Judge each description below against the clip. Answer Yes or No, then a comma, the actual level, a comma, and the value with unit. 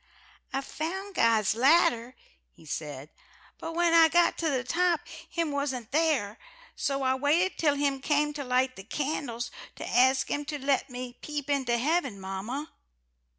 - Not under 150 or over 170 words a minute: Yes, average, 160 wpm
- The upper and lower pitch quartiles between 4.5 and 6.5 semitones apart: No, average, 4.1 semitones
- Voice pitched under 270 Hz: No, very high, 275 Hz